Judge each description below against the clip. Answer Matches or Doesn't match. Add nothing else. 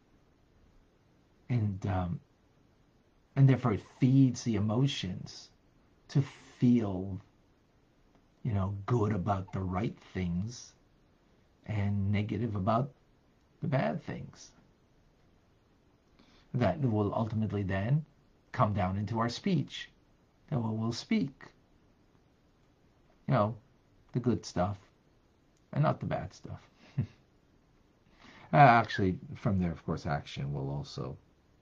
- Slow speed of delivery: Matches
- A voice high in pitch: Doesn't match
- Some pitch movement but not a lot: Matches